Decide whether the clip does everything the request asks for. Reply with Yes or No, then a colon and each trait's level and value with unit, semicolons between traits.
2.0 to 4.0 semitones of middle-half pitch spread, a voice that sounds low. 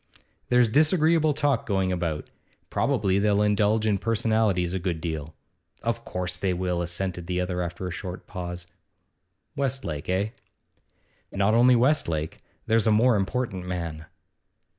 No: average, 4.4 semitones; very low, 95 Hz